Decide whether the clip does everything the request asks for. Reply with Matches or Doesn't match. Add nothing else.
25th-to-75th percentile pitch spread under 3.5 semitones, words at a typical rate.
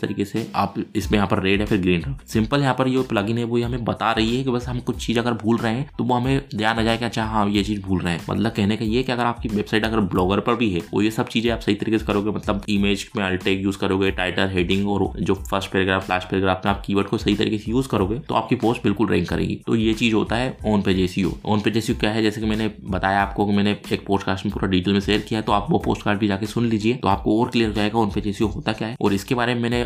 Doesn't match